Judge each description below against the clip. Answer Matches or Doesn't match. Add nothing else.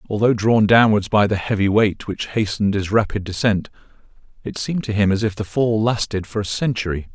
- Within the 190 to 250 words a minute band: Matches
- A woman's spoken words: Doesn't match